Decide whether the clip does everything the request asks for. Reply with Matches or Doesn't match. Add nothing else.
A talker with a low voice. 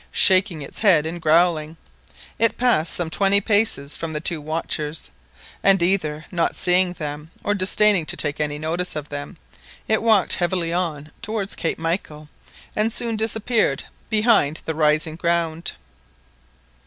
Doesn't match